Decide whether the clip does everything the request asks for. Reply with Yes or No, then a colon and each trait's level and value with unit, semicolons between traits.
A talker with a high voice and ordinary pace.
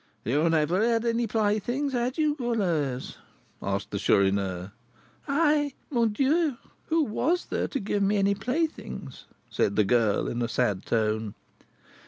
Yes: high, 210 Hz; average, 150 wpm